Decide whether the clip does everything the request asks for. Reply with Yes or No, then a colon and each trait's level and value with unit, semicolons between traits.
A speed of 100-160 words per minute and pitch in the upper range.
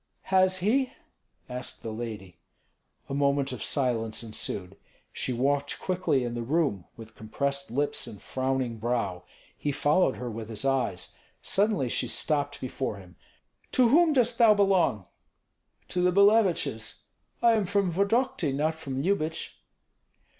No: average, 140 wpm; medium, 140 Hz